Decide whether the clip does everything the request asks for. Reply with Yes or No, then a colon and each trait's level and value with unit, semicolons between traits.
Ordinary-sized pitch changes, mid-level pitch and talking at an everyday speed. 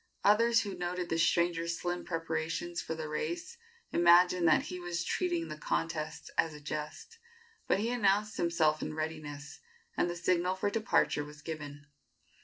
Yes: average, 3.0 semitones; medium, 170 Hz; average, 160 wpm